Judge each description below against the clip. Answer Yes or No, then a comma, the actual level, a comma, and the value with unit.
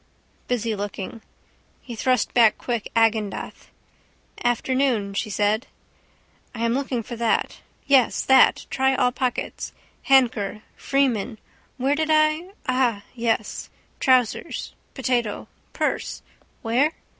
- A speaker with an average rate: No, slow, 110 wpm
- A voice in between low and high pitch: No, high, 240 Hz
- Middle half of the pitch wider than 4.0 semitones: No, average, 3.2 semitones